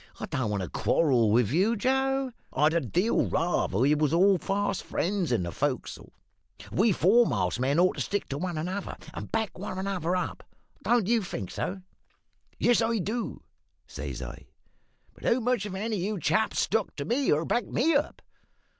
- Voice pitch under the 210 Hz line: Yes, medium, 185 Hz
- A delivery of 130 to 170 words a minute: No, average, 185 wpm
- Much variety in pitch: Yes, wide, 6.9 semitones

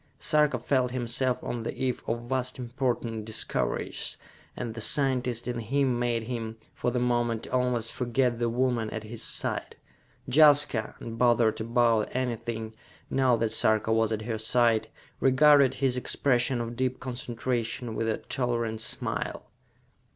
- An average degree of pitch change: No, narrow, 2.0 semitones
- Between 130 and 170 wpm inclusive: Yes, average, 145 wpm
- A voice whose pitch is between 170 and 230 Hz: No, low, 120 Hz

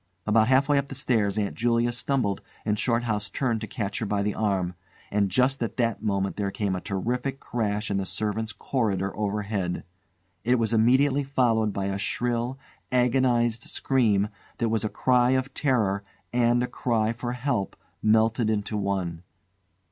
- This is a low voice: Yes, low, 110 Hz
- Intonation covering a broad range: No, average, 3.2 semitones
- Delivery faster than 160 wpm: Yes, average, 170 wpm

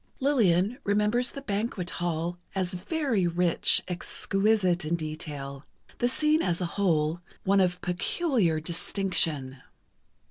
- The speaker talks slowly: Yes, slow, 110 wpm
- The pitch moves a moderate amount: Yes, average, 4.0 semitones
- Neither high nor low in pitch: Yes, medium, 180 Hz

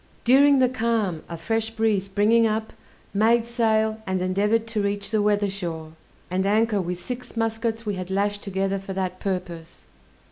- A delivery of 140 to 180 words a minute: Yes, average, 170 wpm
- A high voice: Yes, high, 205 Hz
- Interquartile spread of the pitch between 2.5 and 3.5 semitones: Yes, average, 2.9 semitones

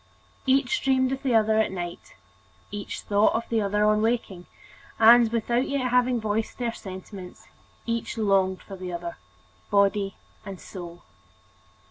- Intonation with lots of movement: No, average, 3.5 semitones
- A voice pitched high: Yes, high, 215 Hz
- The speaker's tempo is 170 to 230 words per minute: No, average, 150 wpm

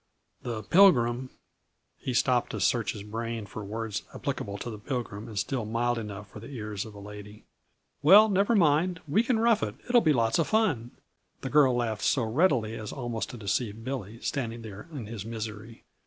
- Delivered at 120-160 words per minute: No, average, 200 wpm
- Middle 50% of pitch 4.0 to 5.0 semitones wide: Yes, average, 4.6 semitones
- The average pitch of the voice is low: Yes, low, 115 Hz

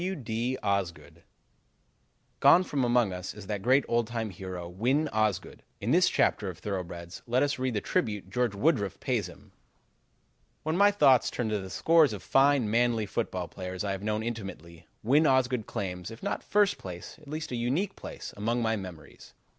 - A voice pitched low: Yes, low, 110 Hz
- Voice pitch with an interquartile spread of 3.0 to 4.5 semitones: No, average, 5.3 semitones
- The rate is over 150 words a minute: Yes, average, 185 wpm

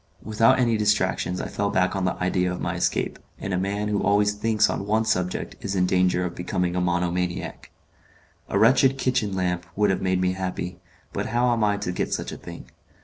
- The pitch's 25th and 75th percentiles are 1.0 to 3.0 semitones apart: Yes, narrow, 2.5 semitones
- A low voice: Yes, very low, 95 Hz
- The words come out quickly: Yes, fast, 210 wpm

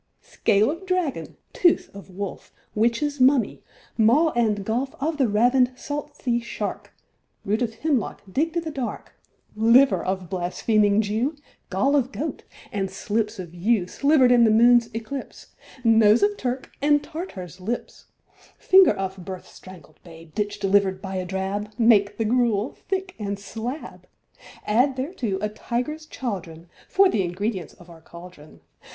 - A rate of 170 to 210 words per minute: No, average, 155 wpm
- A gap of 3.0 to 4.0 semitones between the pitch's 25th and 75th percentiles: No, wide, 5.6 semitones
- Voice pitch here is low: No, high, 225 Hz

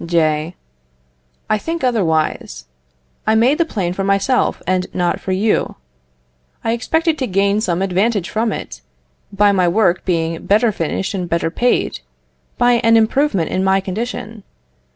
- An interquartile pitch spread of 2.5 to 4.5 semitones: Yes, average, 4.2 semitones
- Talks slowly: No, average, 150 wpm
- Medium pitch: No, high, 200 Hz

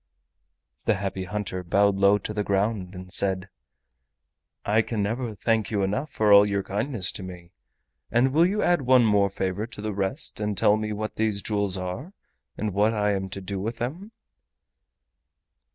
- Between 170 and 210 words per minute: Yes, average, 185 wpm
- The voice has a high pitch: No, low, 105 Hz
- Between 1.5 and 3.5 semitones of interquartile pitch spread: Yes, narrow, 2.4 semitones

